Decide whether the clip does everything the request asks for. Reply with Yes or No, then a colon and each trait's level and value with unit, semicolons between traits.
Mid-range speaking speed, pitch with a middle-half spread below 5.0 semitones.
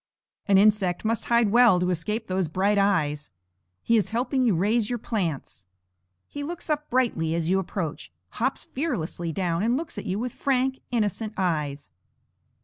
No: average, 165 wpm; wide, 5.4 semitones